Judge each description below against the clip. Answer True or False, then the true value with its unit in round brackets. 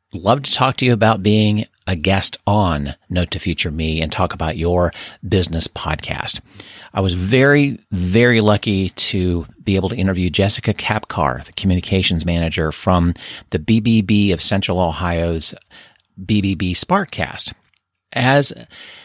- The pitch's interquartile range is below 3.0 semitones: False (3.6 semitones)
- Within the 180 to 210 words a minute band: False (140 wpm)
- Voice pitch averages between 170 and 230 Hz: False (95 Hz)